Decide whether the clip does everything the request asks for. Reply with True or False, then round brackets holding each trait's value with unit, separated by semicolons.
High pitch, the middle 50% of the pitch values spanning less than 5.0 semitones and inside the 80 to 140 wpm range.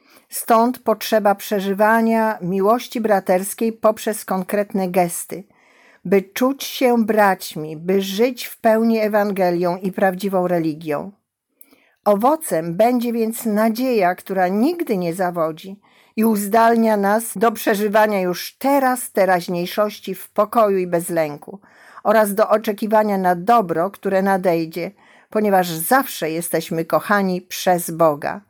True (205 Hz; 3.7 semitones; 115 wpm)